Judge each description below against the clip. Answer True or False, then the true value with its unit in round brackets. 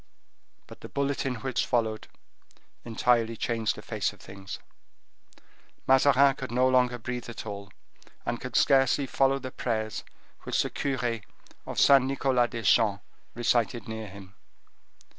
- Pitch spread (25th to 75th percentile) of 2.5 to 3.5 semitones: True (3.0 semitones)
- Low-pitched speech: True (120 Hz)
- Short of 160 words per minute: True (140 wpm)